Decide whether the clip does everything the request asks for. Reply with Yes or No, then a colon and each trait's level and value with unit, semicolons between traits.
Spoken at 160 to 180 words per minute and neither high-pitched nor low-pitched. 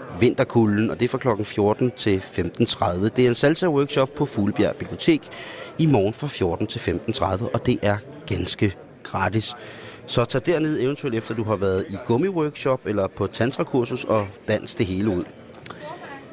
No: average, 170 wpm; low, 115 Hz